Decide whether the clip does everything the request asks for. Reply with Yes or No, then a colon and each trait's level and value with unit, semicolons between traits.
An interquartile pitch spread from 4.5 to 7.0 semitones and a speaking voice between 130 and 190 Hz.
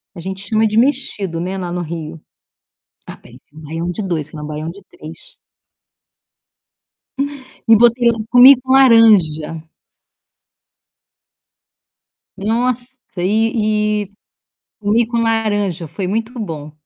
No: wide, 5.4 semitones; high, 205 Hz